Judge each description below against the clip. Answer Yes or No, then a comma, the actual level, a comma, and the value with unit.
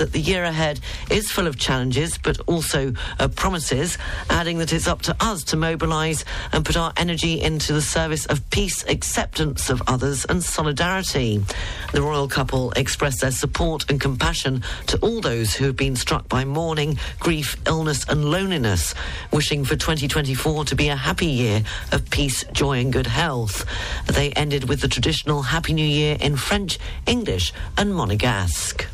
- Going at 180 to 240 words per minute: No, average, 170 wpm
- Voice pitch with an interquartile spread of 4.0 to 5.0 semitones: Yes, average, 4.3 semitones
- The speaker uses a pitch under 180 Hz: Yes, medium, 140 Hz